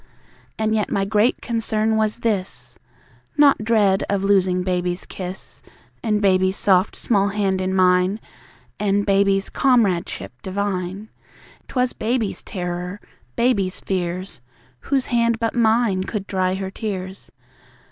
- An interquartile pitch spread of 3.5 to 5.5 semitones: No, average, 2.7 semitones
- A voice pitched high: Yes, high, 200 Hz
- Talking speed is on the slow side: Yes, slow, 125 wpm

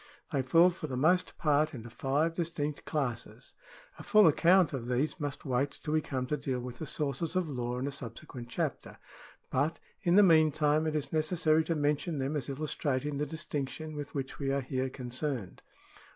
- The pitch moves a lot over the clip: No, average, 3.0 semitones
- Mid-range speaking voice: Yes, medium, 145 Hz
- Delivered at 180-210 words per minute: Yes, average, 195 wpm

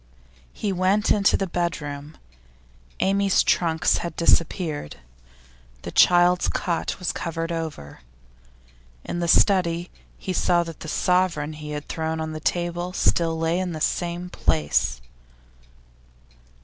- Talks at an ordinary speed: No, slow, 130 wpm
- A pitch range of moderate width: No, narrow, 2.1 semitones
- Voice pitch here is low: No, medium, 170 Hz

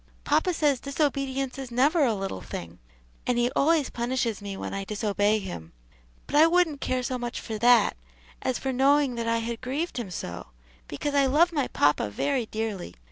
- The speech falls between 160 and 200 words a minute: Yes, average, 190 wpm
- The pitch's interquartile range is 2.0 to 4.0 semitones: No, average, 4.6 semitones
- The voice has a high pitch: Yes, very high, 250 Hz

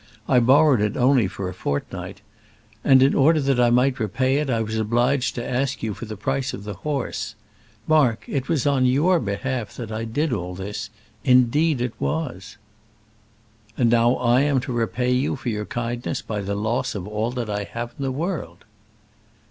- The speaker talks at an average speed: Yes, average, 190 wpm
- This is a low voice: Yes, low, 120 Hz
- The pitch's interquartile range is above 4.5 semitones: No, average, 3.7 semitones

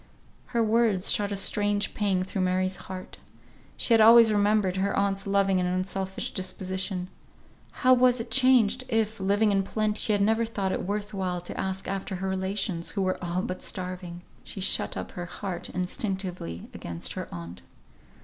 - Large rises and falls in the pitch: No, narrow, 2.4 semitones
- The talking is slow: No, average, 175 wpm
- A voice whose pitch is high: Yes, high, 195 Hz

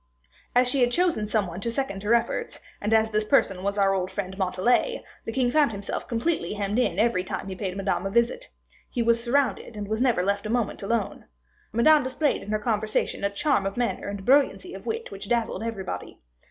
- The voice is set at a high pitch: Yes, high, 220 Hz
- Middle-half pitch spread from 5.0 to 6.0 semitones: No, average, 3.8 semitones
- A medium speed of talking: No, fast, 215 wpm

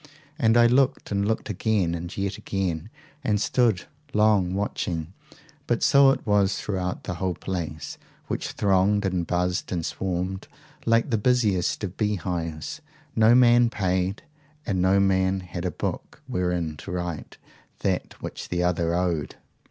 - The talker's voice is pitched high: No, very low, 95 Hz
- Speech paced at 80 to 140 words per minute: No, average, 150 wpm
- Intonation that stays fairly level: No, average, 3.1 semitones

